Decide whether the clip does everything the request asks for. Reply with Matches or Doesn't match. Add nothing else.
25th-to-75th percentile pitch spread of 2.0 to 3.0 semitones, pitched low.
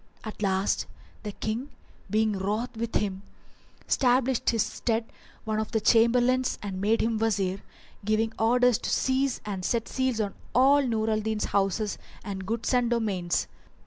Doesn't match